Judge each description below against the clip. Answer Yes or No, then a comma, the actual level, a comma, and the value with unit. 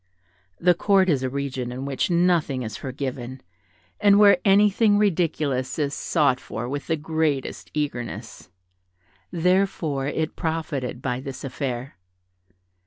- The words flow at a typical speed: No, slow, 125 wpm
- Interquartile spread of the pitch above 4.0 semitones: Yes, average, 5.0 semitones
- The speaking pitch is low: No, medium, 145 Hz